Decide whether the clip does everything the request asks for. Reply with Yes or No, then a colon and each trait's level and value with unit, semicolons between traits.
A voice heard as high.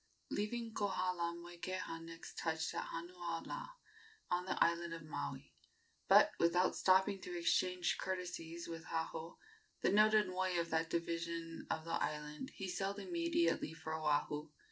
No: medium, 170 Hz